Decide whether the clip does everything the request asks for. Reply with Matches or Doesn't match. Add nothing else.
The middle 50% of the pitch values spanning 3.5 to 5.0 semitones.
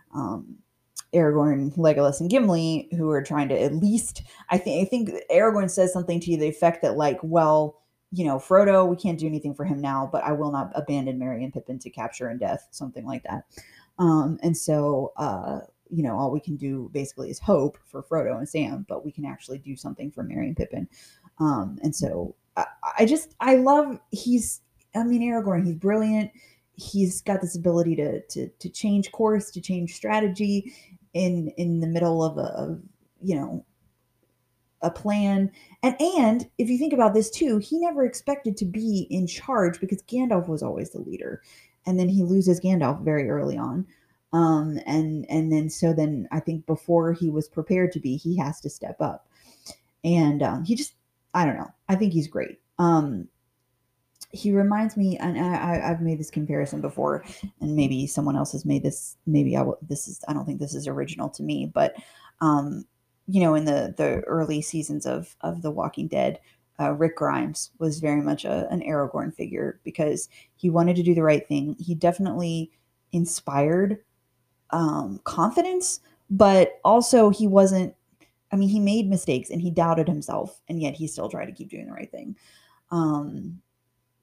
Matches